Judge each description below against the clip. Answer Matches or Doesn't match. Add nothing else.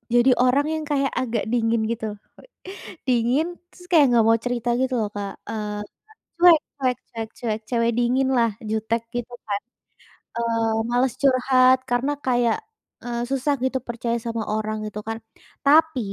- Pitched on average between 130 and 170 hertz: Doesn't match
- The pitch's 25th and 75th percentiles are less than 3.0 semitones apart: Matches